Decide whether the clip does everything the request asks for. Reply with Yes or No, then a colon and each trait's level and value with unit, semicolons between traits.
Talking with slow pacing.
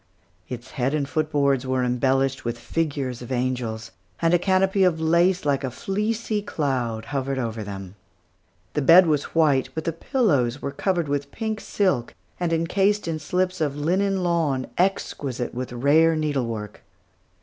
No: average, 160 wpm